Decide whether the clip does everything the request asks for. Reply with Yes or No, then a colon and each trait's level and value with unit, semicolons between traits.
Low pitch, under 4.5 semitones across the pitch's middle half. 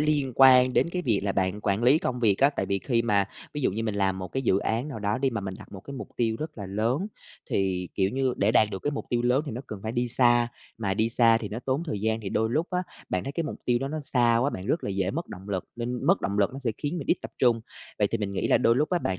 No: low, 115 Hz; average, 4.8 semitones